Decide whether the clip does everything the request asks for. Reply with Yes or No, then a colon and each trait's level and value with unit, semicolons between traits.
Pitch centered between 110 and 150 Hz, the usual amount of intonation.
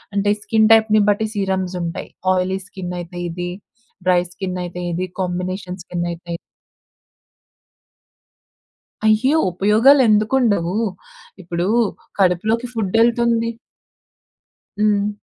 No: high, 190 Hz; average, 3.4 semitones